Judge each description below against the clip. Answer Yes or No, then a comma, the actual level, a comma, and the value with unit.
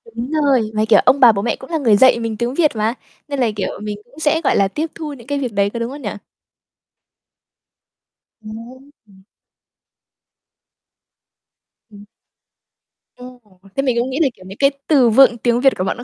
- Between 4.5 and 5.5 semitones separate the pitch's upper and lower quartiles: No, average, 4.1 semitones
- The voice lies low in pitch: No, high, 245 Hz